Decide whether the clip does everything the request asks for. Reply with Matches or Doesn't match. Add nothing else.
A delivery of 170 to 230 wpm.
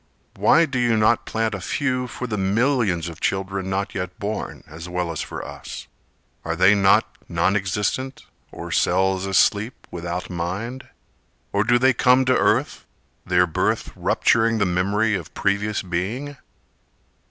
Doesn't match